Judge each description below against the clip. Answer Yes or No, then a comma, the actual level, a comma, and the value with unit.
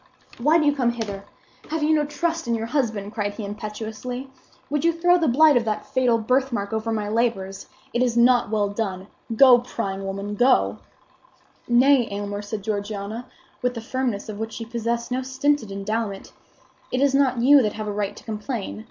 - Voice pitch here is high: Yes, high, 230 Hz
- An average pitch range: Yes, average, 3.9 semitones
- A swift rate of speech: No, average, 190 wpm